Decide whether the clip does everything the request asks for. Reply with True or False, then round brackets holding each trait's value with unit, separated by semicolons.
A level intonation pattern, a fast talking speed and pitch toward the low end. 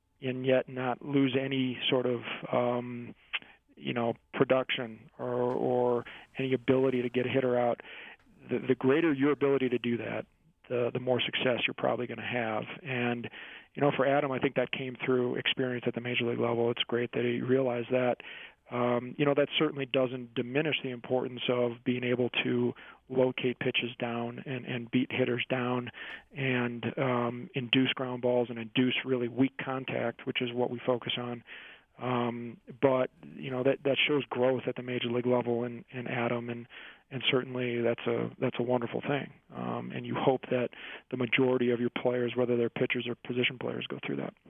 False (1.4 semitones; 185 wpm; 125 Hz)